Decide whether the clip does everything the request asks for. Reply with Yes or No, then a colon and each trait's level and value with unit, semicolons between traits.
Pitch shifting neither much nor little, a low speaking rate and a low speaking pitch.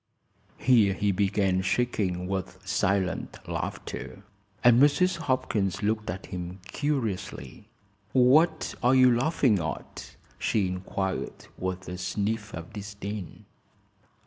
Yes: average, 4.8 semitones; slow, 110 wpm; low, 100 Hz